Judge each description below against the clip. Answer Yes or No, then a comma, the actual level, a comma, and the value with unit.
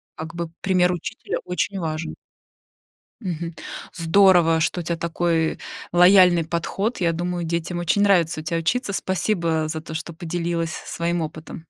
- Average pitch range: No, narrow, 1.7 semitones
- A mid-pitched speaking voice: Yes, medium, 170 Hz